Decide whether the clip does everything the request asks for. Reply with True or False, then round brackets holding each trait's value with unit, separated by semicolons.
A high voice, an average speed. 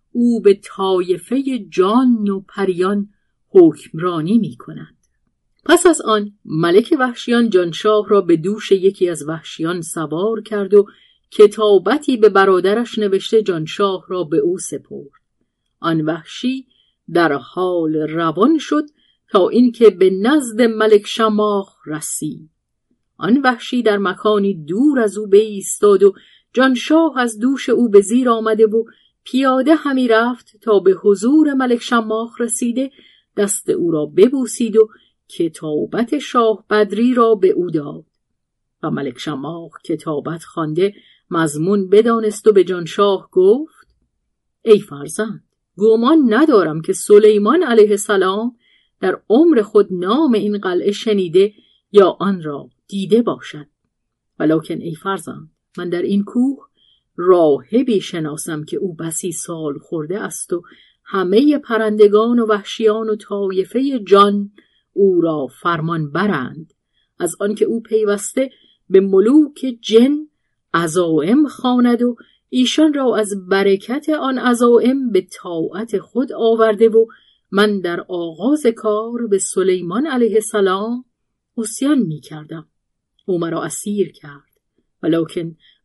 True (210 Hz; 125 wpm)